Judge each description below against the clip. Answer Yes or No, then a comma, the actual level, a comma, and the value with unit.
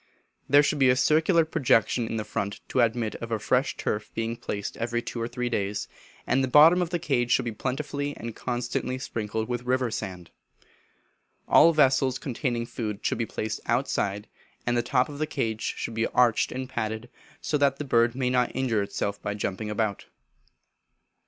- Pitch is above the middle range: No, low, 120 Hz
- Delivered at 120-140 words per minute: No, average, 185 wpm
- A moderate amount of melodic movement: Yes, average, 3.1 semitones